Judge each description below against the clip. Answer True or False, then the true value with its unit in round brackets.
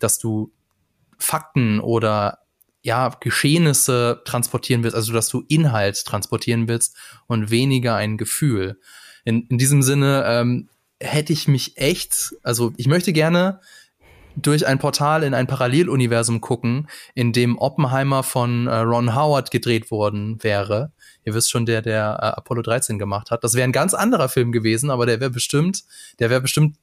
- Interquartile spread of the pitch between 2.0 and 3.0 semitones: False (3.6 semitones)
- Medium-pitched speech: False (125 Hz)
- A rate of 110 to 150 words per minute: False (160 wpm)